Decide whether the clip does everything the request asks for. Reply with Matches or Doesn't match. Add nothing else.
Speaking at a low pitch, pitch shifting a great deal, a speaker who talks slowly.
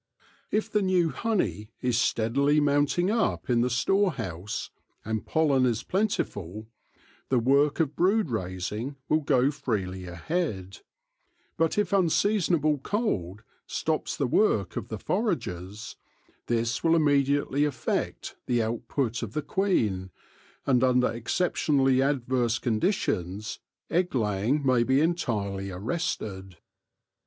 Matches